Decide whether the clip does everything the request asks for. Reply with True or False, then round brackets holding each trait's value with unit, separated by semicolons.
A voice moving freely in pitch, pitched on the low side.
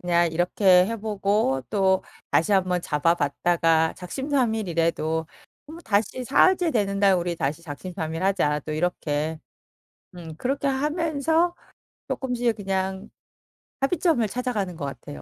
False (6.7 semitones; 190 Hz)